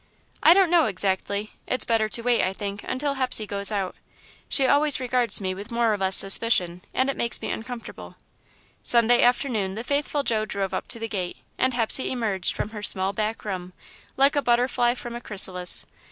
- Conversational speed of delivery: Yes, average, 195 wpm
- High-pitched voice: Yes, high, 225 Hz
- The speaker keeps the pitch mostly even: No, average, 4.1 semitones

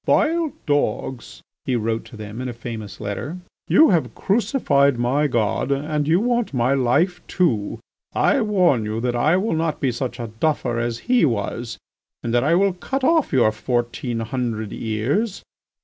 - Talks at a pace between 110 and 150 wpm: No, average, 170 wpm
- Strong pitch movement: Yes, wide, 6.8 semitones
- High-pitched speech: No, low, 130 Hz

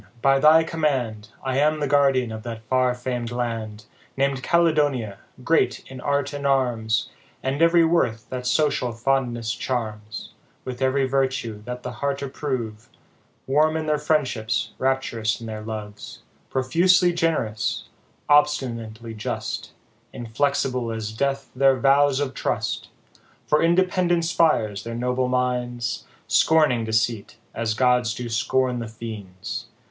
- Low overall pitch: Yes, low, 125 Hz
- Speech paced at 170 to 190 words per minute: No, slow, 135 wpm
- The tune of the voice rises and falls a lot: No, average, 3.9 semitones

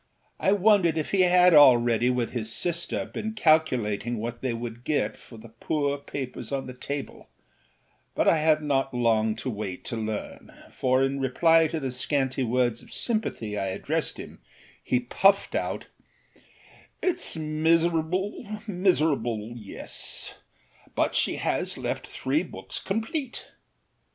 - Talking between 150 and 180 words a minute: No, average, 140 wpm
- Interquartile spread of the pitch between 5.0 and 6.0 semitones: Yes, wide, 5.6 semitones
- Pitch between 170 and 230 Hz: No, low, 135 Hz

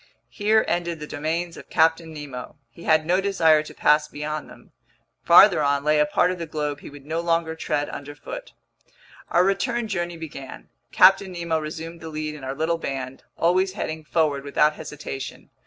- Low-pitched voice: No, medium, 160 Hz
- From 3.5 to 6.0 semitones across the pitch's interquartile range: No, narrow, 2.5 semitones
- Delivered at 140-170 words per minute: No, average, 180 wpm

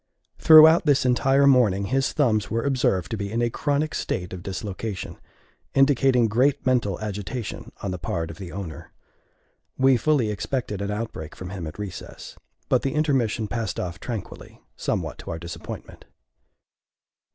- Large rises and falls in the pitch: Yes, wide, 5.8 semitones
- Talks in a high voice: No, low, 110 Hz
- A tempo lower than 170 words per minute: Yes, average, 155 wpm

